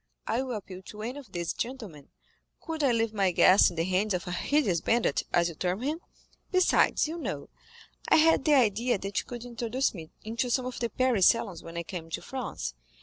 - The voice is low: No, high, 225 Hz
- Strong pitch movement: Yes, wide, 5.8 semitones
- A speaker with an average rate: No, fast, 215 wpm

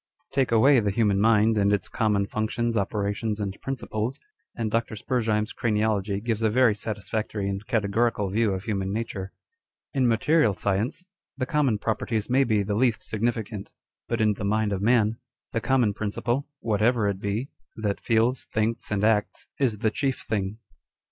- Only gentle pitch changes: Yes, narrow, 2.3 semitones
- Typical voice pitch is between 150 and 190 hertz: No, low, 110 Hz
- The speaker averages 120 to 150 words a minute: No, average, 170 wpm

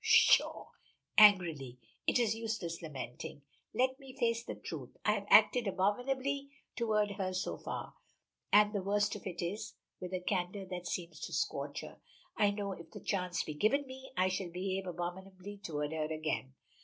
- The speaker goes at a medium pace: Yes, average, 170 wpm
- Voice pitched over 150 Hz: Yes, high, 190 Hz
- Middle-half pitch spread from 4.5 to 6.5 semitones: No, average, 3.8 semitones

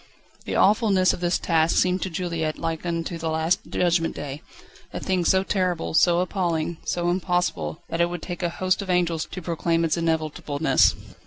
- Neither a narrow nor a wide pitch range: No, narrow, 1.9 semitones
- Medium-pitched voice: Yes, medium, 170 Hz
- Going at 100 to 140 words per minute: No, average, 180 wpm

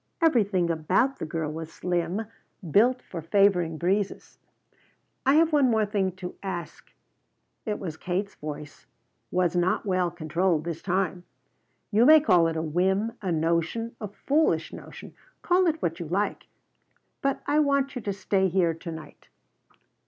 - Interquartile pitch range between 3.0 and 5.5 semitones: Yes, average, 5.0 semitones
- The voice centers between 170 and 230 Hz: Yes, medium, 185 Hz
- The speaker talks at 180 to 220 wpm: No, average, 150 wpm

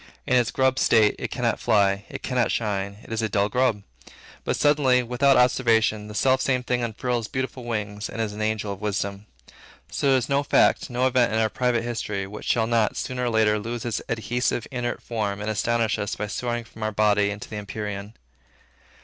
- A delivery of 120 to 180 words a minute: No, average, 200 wpm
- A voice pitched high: No, low, 115 Hz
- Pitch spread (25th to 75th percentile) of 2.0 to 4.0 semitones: Yes, average, 2.8 semitones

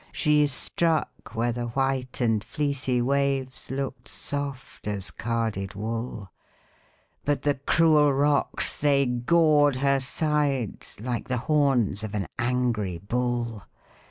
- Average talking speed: No, slow, 120 wpm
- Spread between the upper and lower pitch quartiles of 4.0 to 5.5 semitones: No, average, 3.6 semitones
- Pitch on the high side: No, low, 130 Hz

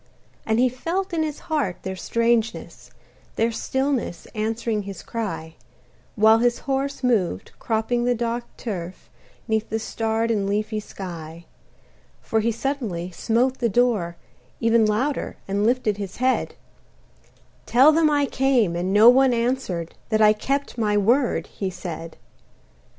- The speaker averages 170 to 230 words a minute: No, average, 140 wpm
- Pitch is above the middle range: Yes, high, 225 Hz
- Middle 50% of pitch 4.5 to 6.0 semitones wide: No, average, 3.7 semitones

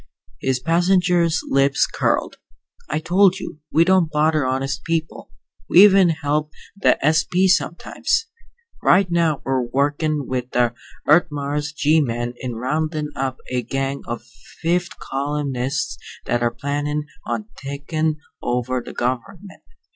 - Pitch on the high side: No, medium, 145 Hz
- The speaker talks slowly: Yes, slow, 130 wpm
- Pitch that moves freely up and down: No, average, 4.1 semitones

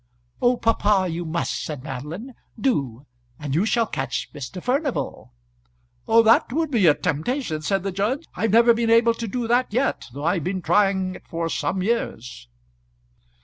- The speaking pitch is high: Yes, high, 195 Hz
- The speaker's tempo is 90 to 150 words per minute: No, average, 165 wpm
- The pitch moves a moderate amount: No, wide, 6.5 semitones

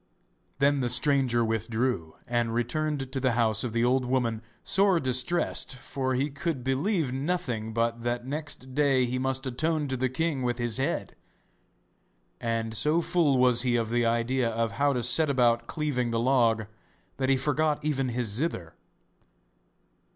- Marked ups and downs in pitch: No, average, 3.1 semitones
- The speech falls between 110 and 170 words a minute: Yes, average, 165 wpm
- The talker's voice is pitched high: No, low, 130 Hz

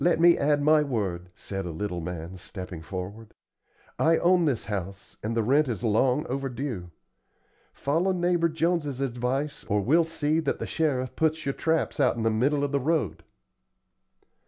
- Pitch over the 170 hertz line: No, low, 135 Hz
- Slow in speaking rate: No, average, 170 wpm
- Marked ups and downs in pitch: Yes, wide, 7.1 semitones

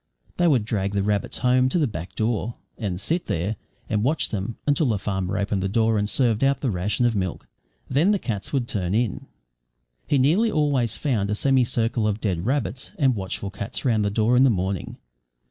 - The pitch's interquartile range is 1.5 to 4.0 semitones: No, average, 4.7 semitones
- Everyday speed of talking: No, fast, 210 wpm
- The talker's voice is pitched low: Yes, low, 110 Hz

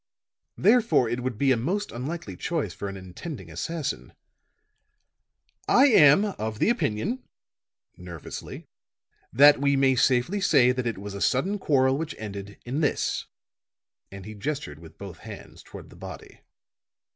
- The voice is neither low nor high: No, low, 130 Hz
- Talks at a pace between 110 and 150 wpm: Yes, average, 145 wpm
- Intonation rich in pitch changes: Yes, wide, 7.8 semitones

